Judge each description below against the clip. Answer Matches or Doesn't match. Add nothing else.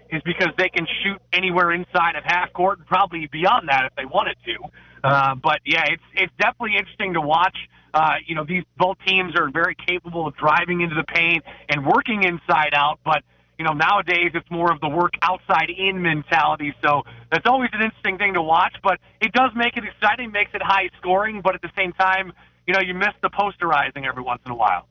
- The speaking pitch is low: Doesn't match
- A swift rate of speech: Matches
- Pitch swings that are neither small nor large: Matches